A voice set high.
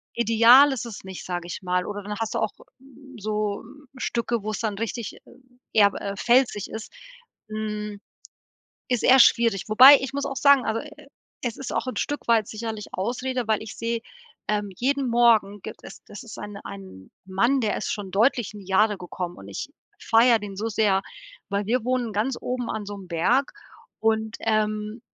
Yes: high, 220 Hz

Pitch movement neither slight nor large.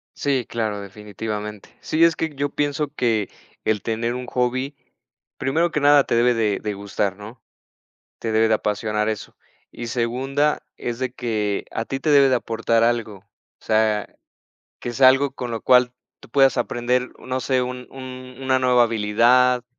Yes: average, 3.0 semitones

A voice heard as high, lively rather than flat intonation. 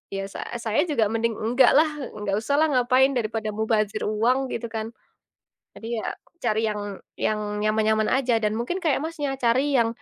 No: high, 230 Hz; average, 3.1 semitones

